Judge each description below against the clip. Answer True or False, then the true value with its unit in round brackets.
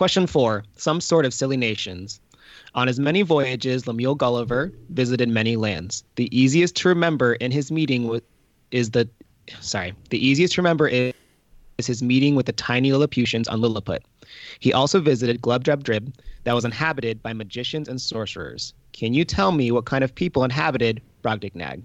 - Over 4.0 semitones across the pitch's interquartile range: False (3.5 semitones)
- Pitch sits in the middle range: False (125 Hz)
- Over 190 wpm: False (170 wpm)